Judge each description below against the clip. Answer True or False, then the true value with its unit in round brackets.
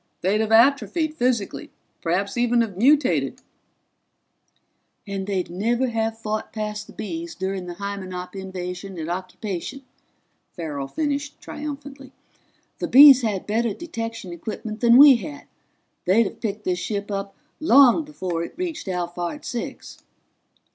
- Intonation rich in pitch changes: True (5.8 semitones)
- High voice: True (215 Hz)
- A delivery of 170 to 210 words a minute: False (135 wpm)